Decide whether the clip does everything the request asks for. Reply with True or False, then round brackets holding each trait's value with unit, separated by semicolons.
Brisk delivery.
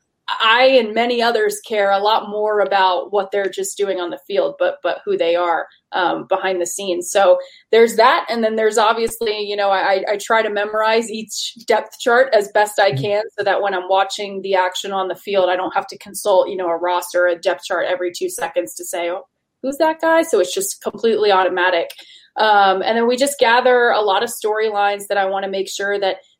True (225 wpm)